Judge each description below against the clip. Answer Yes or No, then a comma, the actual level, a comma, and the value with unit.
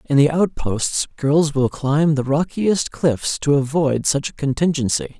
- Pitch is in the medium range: Yes, medium, 145 Hz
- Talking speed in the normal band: Yes, average, 160 wpm